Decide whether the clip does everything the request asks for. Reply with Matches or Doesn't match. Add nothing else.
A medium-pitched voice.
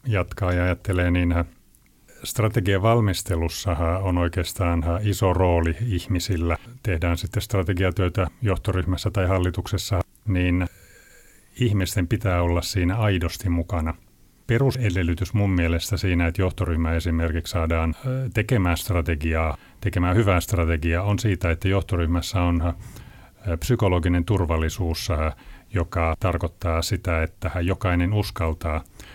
Doesn't match